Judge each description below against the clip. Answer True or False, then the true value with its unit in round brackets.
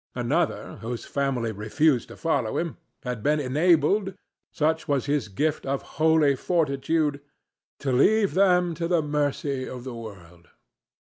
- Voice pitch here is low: False (145 Hz)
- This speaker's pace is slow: True (130 wpm)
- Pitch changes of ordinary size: True (4.1 semitones)